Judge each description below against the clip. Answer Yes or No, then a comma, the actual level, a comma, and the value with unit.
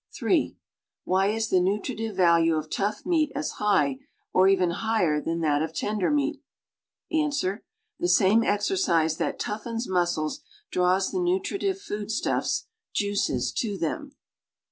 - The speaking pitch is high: Yes, high, 205 Hz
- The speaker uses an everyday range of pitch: No, wide, 8.0 semitones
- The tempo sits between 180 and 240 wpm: No, average, 140 wpm